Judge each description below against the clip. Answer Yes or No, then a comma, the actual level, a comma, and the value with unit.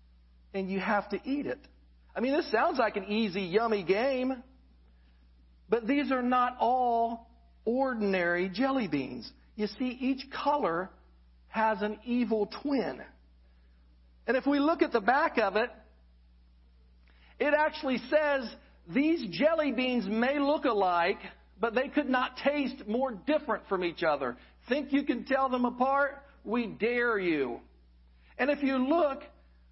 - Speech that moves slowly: No, average, 145 wpm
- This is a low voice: No, high, 230 Hz